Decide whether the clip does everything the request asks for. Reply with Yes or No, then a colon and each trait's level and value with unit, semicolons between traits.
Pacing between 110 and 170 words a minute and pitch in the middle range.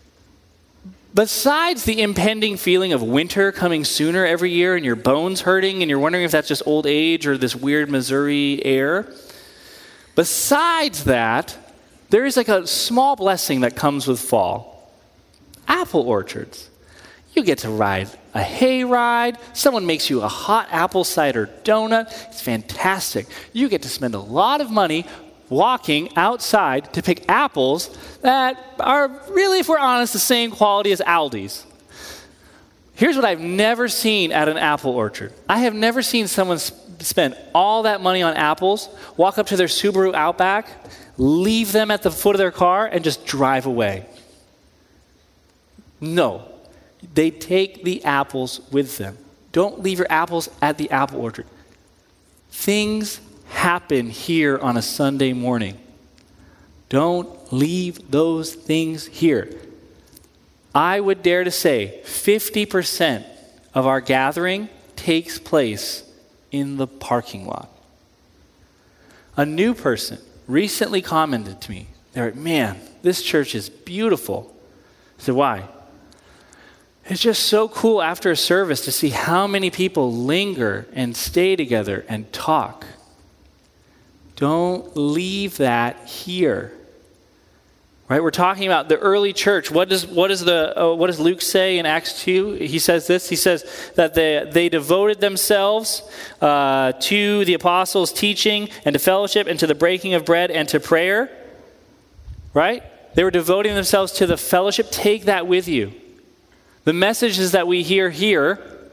Yes: average, 145 wpm; medium, 170 Hz